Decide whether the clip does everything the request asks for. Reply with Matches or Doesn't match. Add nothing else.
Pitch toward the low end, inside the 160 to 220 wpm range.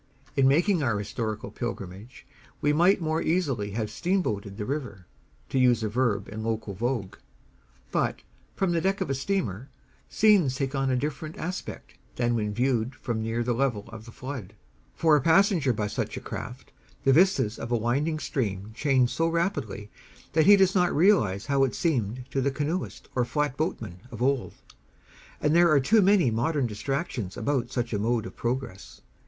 Matches